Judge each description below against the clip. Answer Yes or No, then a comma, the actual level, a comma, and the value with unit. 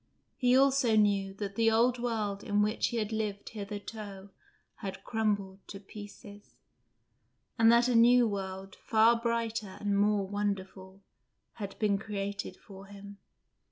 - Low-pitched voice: No, high, 205 Hz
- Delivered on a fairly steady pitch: Yes, narrow, 2.2 semitones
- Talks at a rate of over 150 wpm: No, average, 140 wpm